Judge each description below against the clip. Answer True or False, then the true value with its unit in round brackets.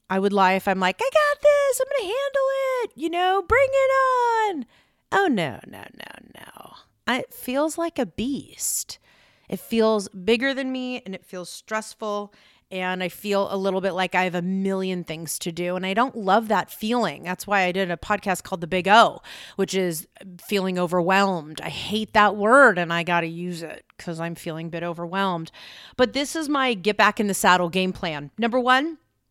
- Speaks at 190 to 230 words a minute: True (205 wpm)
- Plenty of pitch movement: True (6.2 semitones)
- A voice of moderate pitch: False (200 Hz)